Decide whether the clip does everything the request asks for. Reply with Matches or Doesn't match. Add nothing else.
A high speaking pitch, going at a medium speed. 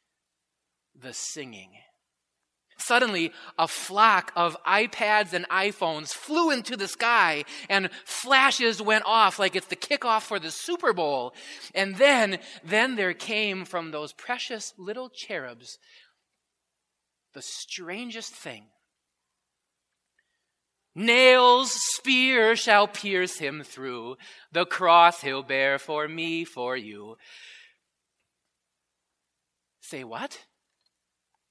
Doesn't match